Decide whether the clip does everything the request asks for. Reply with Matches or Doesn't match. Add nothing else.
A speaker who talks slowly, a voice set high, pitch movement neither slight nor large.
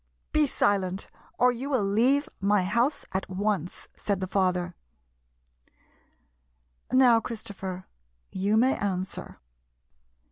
Matches